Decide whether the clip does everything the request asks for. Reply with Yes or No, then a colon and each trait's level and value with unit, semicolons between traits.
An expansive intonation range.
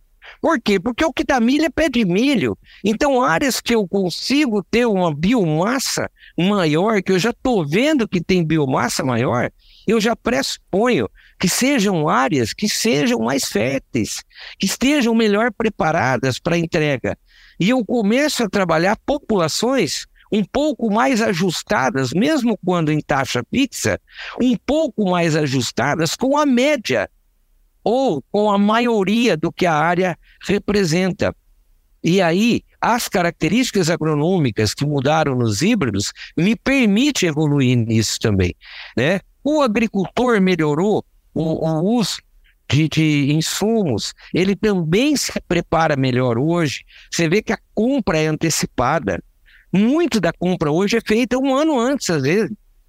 Yes: wide, 6.9 semitones